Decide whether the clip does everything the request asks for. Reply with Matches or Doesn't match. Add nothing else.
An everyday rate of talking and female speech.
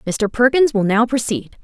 Matches